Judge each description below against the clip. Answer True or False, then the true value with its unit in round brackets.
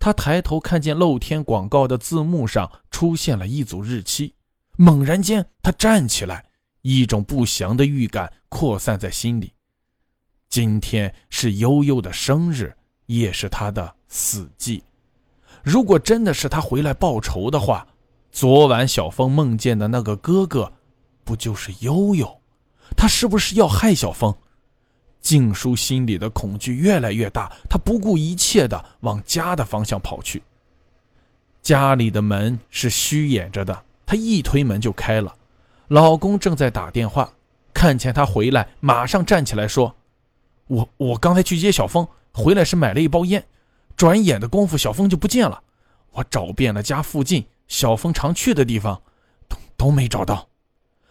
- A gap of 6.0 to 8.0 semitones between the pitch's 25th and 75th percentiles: True (7.0 semitones)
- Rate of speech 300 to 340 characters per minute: False (225 characters per minute)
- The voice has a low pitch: True (130 Hz)